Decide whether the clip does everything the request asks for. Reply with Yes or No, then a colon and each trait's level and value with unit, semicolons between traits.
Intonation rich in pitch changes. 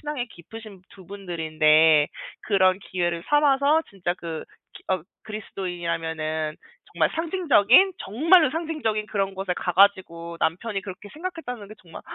Yes: wide, 6.7 semitones